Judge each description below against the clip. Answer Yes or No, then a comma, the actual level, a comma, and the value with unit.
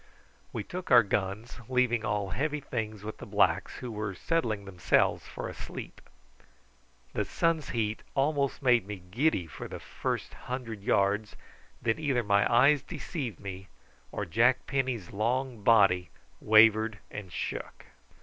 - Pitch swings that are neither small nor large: Yes, average, 4.1 semitones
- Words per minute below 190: Yes, average, 145 wpm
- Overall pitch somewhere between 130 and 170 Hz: No, low, 110 Hz